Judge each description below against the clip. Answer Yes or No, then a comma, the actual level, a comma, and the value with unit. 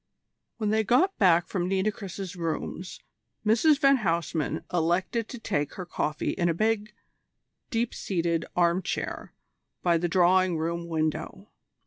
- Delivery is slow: Yes, slow, 130 wpm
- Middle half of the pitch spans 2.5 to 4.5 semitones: Yes, average, 3.9 semitones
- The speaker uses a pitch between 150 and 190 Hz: Yes, medium, 185 Hz